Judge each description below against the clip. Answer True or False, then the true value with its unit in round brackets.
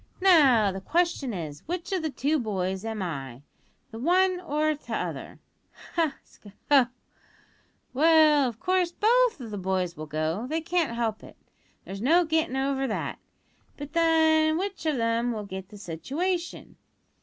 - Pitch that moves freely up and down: True (8.0 semitones)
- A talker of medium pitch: False (275 Hz)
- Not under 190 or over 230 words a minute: False (160 wpm)